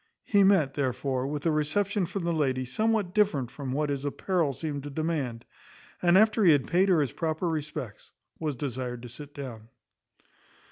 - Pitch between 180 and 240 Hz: No, medium, 150 Hz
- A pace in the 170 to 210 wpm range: Yes, average, 180 wpm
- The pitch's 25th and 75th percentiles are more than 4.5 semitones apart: Yes, average, 4.9 semitones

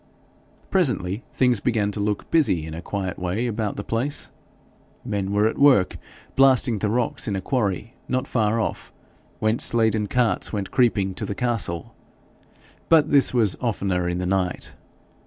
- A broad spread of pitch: No, average, 4.1 semitones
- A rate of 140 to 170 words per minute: Yes, average, 160 wpm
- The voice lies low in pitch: Yes, low, 110 Hz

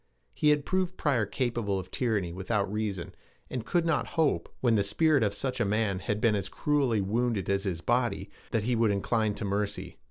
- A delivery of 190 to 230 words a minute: Yes, average, 200 wpm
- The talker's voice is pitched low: Yes, low, 110 Hz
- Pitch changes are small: No, average, 4.3 semitones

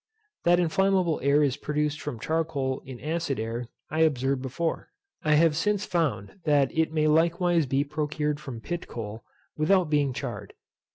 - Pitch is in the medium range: Yes, medium, 150 Hz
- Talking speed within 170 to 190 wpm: No, average, 160 wpm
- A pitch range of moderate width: Yes, average, 3.4 semitones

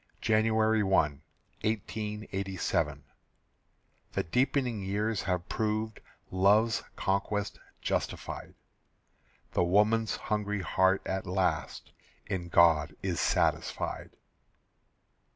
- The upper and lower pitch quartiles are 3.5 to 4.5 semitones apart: No, narrow, 2.5 semitones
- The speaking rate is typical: No, slow, 80 wpm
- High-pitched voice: No, low, 100 Hz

